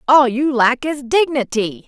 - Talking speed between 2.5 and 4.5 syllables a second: Yes, 4.1 syllables/s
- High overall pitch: Yes, very high, 260 Hz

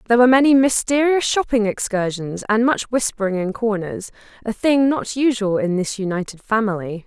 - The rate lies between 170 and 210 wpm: No, average, 155 wpm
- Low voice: No, high, 220 Hz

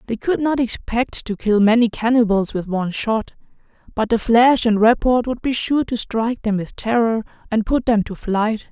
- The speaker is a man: No, female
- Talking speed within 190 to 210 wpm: Yes, average, 200 wpm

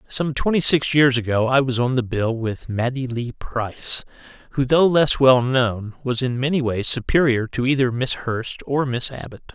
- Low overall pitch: Yes, low, 125 Hz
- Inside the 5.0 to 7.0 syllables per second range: No, 4.6 syllables/s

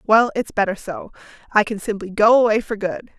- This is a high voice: Yes, high, 215 Hz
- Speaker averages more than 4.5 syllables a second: Yes, 5.4 syllables/s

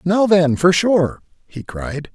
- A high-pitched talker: No, medium, 165 Hz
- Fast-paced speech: No, average, 170 wpm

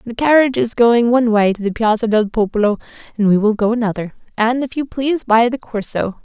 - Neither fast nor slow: No, fast, 220 wpm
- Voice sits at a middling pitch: No, high, 225 Hz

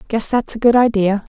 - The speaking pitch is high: Yes, high, 220 Hz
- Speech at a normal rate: No, fast, 265 wpm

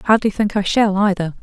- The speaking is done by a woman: Yes, female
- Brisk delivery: Yes, fast, 210 wpm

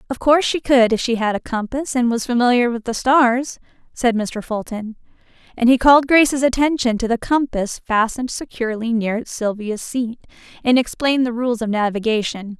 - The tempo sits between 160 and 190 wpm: Yes, average, 175 wpm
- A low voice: No, high, 240 Hz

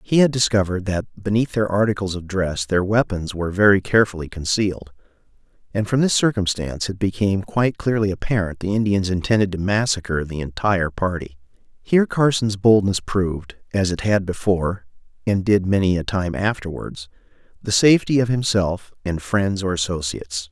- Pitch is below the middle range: Yes, low, 100 Hz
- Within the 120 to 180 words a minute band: Yes, average, 160 wpm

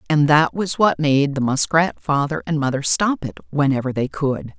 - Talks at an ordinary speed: Yes, average, 195 wpm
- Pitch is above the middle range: No, low, 135 Hz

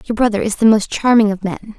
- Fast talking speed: Yes, fast, 270 wpm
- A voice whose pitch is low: No, high, 215 Hz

